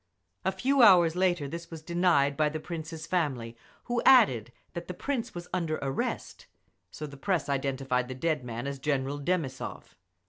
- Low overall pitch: No, medium, 155 Hz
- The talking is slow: No, average, 170 wpm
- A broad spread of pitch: No, average, 4.6 semitones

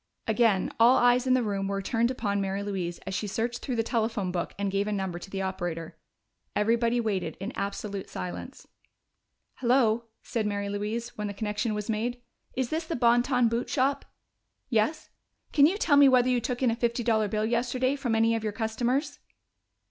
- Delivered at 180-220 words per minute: Yes, average, 195 wpm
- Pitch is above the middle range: Yes, high, 225 Hz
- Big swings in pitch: No, average, 3.3 semitones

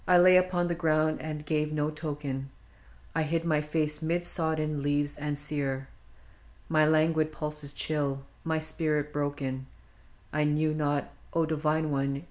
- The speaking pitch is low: No, medium, 150 Hz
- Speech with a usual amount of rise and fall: No, narrow, 1.4 semitones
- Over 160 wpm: No, average, 155 wpm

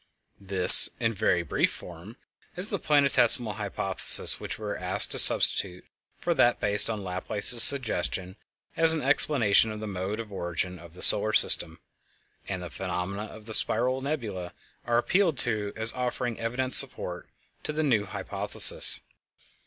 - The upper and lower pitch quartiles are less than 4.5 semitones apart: No, average, 5.1 semitones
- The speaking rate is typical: Yes, average, 155 wpm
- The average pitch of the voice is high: No, low, 110 Hz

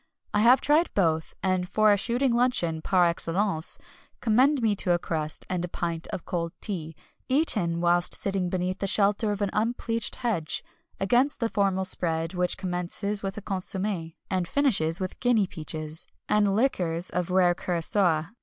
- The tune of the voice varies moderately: Yes, average, 3.8 semitones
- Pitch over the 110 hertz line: Yes, high, 190 Hz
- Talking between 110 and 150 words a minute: No, average, 165 wpm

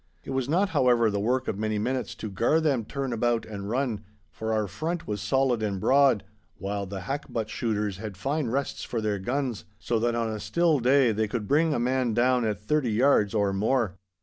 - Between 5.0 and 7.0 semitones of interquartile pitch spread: No, average, 4.0 semitones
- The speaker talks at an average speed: No, fast, 210 wpm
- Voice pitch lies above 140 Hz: No, low, 115 Hz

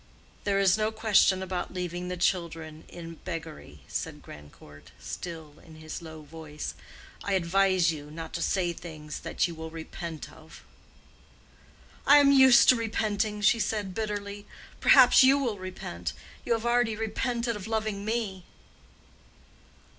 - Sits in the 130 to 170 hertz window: No, medium, 185 Hz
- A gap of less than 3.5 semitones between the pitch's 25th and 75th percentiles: No, average, 5.1 semitones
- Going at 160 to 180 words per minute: No, average, 145 wpm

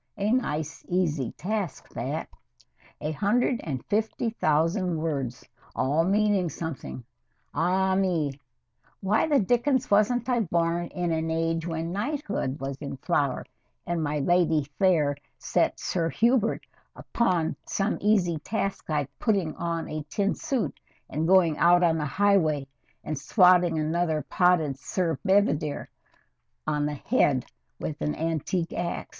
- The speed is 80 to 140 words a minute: Yes, slow, 135 wpm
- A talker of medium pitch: Yes, medium, 170 Hz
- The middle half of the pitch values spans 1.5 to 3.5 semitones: No, average, 4.3 semitones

